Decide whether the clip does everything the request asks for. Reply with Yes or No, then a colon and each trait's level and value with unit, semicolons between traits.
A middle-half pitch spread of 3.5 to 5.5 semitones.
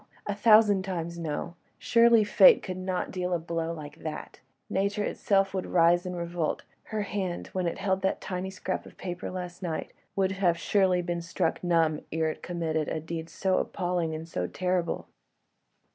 No: narrow, 2.4 semitones